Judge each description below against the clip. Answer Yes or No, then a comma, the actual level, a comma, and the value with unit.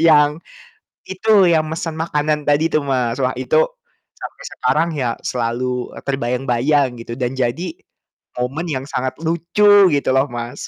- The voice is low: No, medium, 145 Hz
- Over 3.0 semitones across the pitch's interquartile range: Yes, average, 4.5 semitones